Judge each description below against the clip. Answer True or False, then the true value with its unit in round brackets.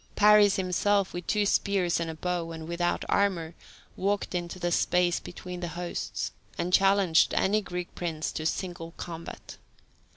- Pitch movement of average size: False (2.3 semitones)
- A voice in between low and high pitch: True (180 Hz)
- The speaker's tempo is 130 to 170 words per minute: True (155 wpm)